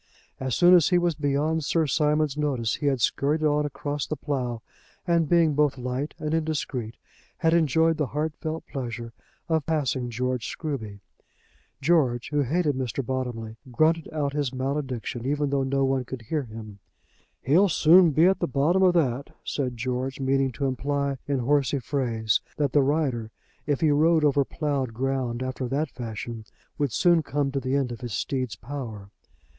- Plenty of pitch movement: No, average, 3.3 semitones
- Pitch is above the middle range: No, medium, 140 Hz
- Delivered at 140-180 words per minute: Yes, average, 170 wpm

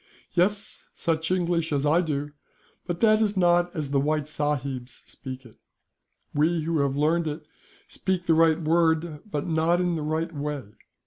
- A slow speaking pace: No, average, 170 wpm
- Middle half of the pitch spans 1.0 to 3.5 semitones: Yes, average, 2.8 semitones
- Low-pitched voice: No, medium, 160 Hz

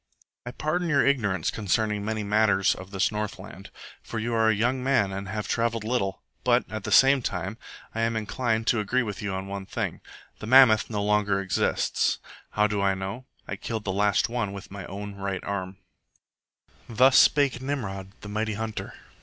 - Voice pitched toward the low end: Yes, low, 105 Hz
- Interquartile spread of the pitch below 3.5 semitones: Yes, average, 3.0 semitones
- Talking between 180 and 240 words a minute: Yes, average, 185 wpm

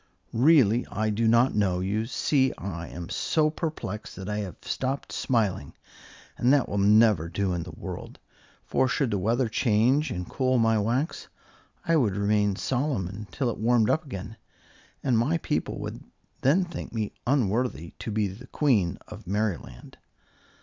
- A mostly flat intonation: No, average, 4.6 semitones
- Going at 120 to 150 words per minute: No, average, 165 wpm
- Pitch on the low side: Yes, low, 110 Hz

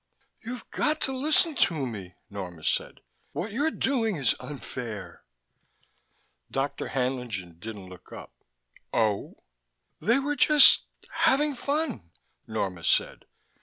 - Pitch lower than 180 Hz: Yes, low, 135 Hz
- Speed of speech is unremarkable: No, slow, 115 wpm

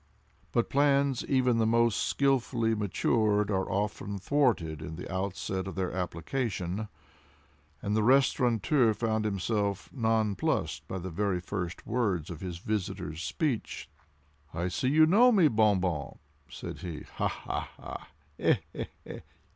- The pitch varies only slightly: No, average, 4.8 semitones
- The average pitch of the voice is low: Yes, low, 105 Hz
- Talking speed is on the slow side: Yes, slow, 130 wpm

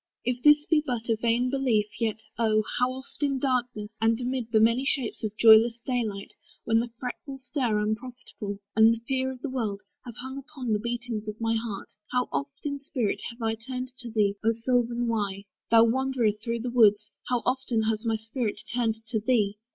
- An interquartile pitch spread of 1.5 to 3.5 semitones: Yes, narrow, 2.5 semitones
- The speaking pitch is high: Yes, high, 235 Hz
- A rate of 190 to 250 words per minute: Yes, average, 200 wpm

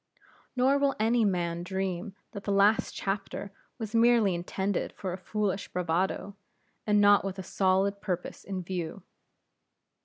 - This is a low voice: No, high, 195 Hz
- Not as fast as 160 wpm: Yes, average, 145 wpm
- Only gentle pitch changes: Yes, narrow, 2.3 semitones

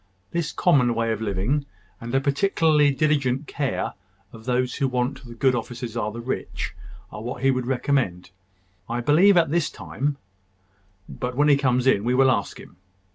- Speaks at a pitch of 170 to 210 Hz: No, low, 130 Hz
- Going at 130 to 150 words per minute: No, average, 180 wpm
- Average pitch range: Yes, average, 3.2 semitones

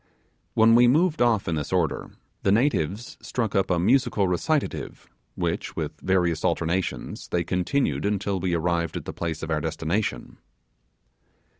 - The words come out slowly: No, average, 150 wpm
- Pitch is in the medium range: No, very low, 95 Hz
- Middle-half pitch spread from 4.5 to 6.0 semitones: Yes, wide, 5.4 semitones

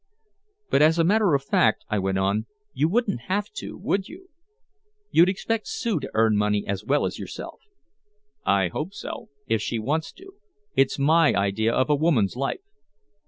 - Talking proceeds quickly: No, average, 175 wpm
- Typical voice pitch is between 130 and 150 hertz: Yes, medium, 140 Hz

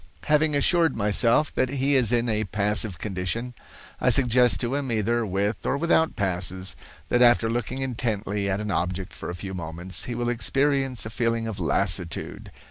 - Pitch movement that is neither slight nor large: Yes, average, 4.3 semitones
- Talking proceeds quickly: No, average, 175 wpm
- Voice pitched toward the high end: No, low, 115 Hz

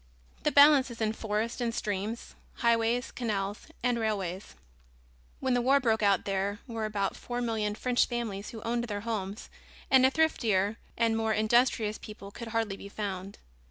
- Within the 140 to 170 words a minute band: Yes, average, 165 wpm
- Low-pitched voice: No, high, 225 Hz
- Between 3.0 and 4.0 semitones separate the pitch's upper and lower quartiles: No, narrow, 2.6 semitones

